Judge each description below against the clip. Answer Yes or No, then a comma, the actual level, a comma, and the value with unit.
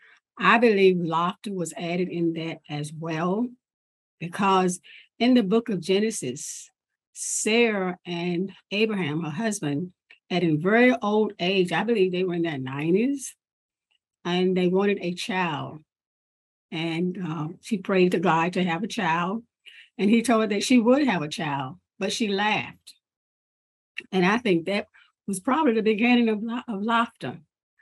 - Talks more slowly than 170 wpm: Yes, average, 155 wpm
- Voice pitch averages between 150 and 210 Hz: Yes, medium, 185 Hz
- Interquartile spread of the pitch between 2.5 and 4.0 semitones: No, average, 4.8 semitones